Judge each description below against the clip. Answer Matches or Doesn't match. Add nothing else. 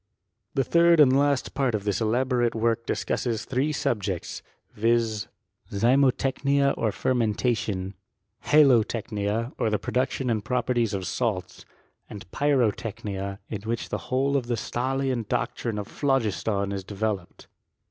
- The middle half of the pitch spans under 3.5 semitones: Doesn't match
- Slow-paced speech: Matches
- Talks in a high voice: Doesn't match